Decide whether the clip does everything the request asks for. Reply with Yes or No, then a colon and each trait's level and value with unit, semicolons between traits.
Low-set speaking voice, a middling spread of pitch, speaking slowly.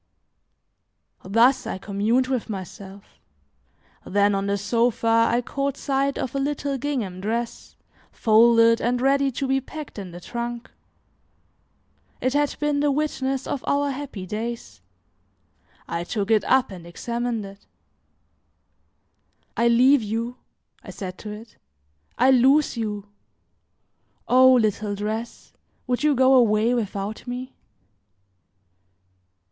No: high, 235 Hz; average, 4.1 semitones; slow, 125 wpm